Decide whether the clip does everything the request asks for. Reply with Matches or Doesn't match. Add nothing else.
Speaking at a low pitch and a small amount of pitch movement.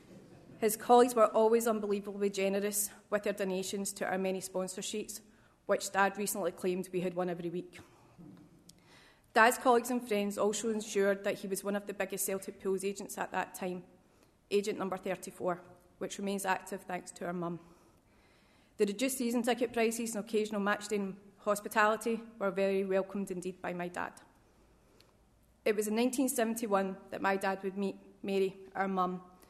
Doesn't match